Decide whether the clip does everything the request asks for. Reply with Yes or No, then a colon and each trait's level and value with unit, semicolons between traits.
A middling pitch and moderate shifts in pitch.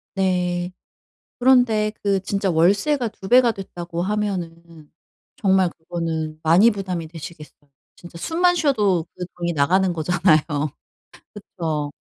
Yes: medium, 180 Hz; average, 3.7 semitones